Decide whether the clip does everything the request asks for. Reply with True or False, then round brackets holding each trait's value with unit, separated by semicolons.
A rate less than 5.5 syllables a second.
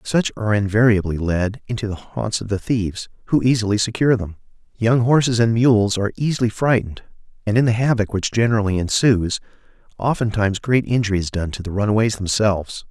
False (6.1 syllables/s)